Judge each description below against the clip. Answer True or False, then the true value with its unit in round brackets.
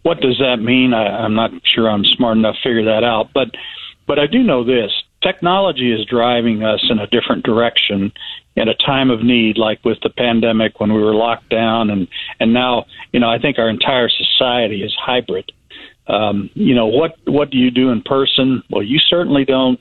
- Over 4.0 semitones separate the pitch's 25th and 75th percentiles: False (3.2 semitones)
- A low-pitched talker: True (120 Hz)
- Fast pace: True (210 wpm)